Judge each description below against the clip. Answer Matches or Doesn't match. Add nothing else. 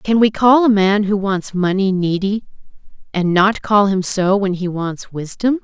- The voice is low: Doesn't match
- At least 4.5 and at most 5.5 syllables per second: Doesn't match